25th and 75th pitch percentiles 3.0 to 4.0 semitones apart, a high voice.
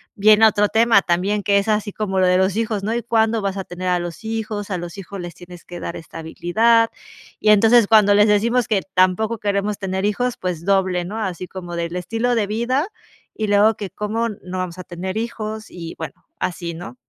Yes: average, 3.3 semitones; high, 200 Hz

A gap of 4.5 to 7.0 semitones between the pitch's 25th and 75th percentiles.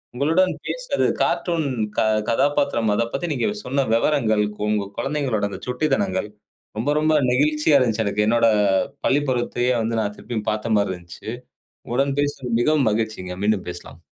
Yes: average, 5.0 semitones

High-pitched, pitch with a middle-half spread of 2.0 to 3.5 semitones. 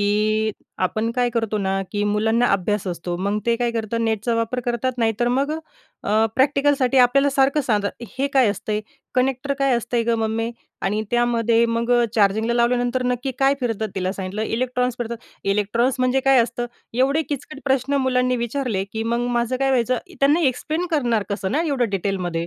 Yes: high, 235 Hz; average, 3.1 semitones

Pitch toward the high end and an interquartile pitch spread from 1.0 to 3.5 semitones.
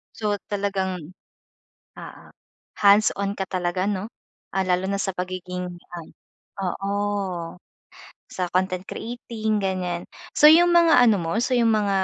Yes: high, 195 Hz; average, 2.8 semitones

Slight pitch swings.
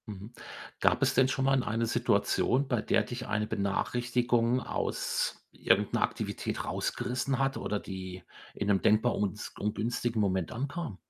No: average, 3.8 semitones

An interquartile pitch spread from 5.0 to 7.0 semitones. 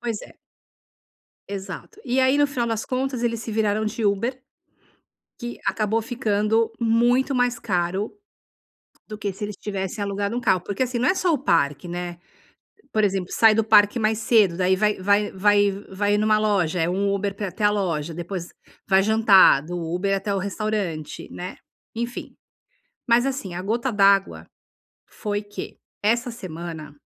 No: average, 3.2 semitones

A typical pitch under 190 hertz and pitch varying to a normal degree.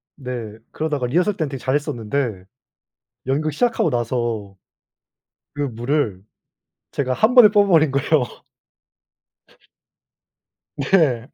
Yes: medium, 140 Hz; average, 4.6 semitones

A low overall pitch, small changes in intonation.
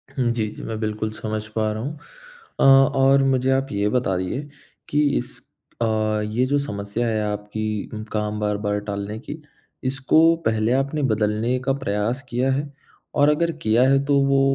No: low, 115 Hz; average, 4.2 semitones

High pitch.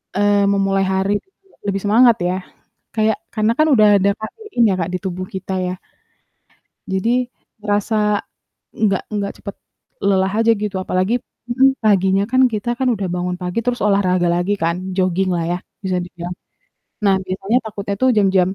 Yes: high, 195 Hz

